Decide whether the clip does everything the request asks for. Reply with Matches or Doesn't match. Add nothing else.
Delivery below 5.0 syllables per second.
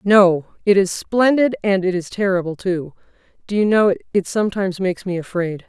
Doesn't match